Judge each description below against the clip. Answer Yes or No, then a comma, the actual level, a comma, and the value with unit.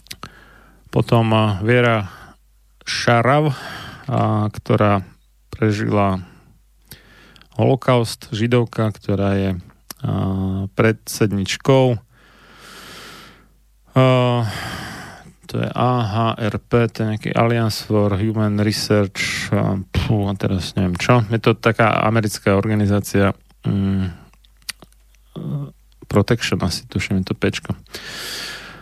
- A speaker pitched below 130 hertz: Yes, low, 110 Hz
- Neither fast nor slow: No, slow, 75 wpm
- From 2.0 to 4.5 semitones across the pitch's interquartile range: Yes, average, 2.9 semitones